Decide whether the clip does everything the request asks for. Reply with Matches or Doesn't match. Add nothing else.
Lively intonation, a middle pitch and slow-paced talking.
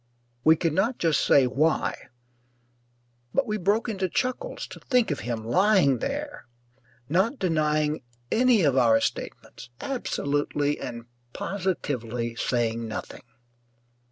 Matches